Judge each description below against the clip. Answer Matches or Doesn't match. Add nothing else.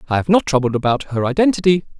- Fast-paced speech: Matches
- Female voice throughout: Doesn't match